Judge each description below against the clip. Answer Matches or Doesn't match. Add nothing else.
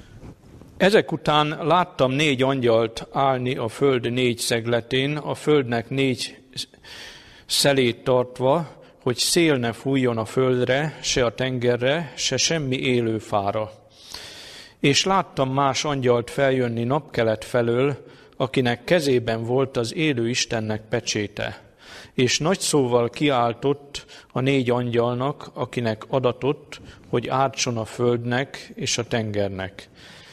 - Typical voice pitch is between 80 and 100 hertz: Doesn't match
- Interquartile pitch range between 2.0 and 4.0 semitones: Matches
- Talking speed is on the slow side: Doesn't match